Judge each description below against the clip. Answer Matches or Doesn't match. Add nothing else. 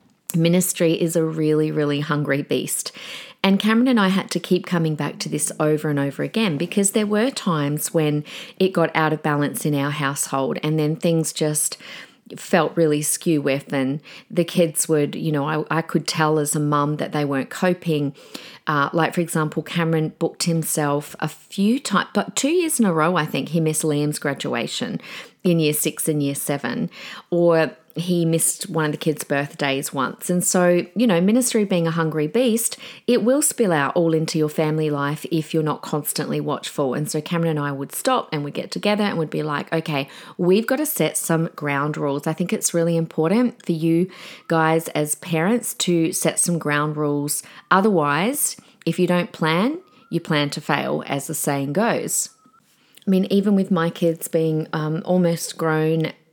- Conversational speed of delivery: Matches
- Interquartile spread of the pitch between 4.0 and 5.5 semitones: Doesn't match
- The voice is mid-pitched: Matches